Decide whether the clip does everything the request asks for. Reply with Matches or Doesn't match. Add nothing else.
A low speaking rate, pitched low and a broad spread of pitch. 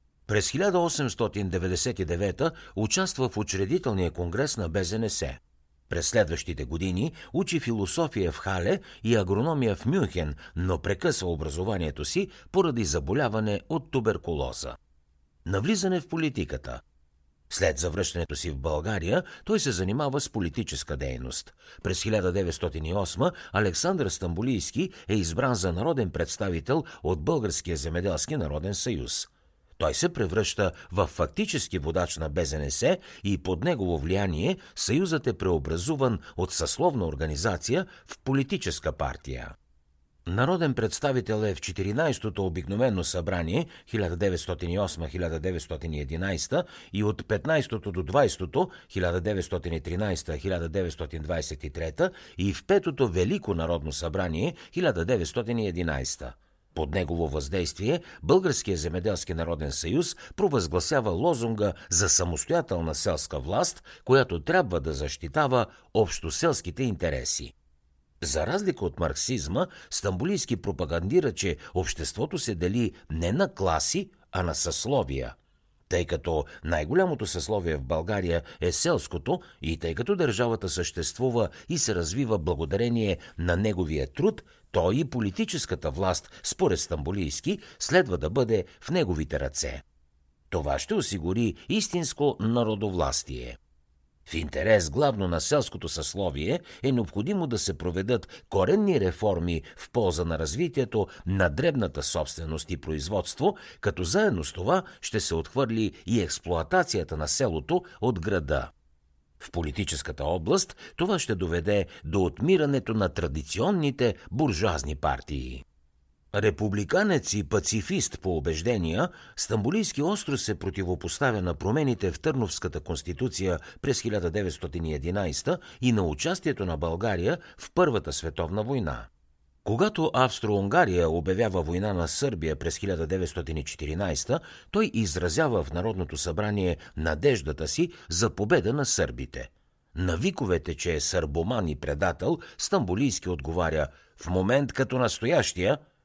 Matches